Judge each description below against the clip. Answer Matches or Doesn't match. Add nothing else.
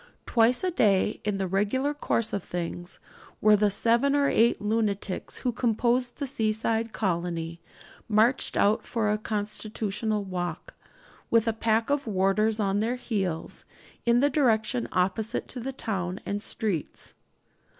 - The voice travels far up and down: Doesn't match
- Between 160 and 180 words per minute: Doesn't match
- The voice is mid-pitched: Doesn't match